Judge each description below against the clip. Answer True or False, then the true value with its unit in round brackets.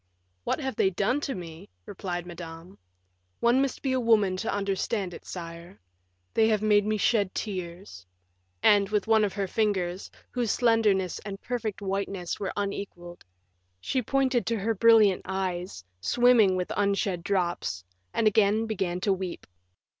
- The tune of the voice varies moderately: True (3.4 semitones)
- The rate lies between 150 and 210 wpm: True (155 wpm)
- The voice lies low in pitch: False (200 Hz)